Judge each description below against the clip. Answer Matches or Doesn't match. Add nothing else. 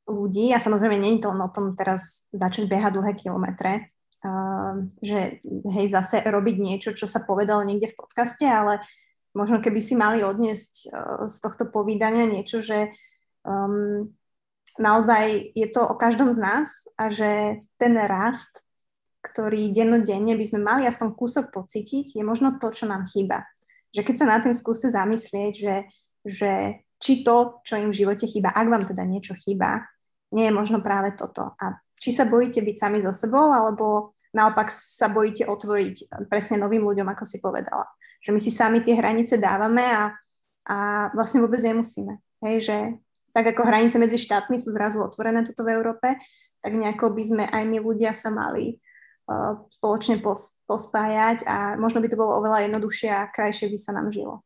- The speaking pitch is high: Matches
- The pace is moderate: Doesn't match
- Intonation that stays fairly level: Matches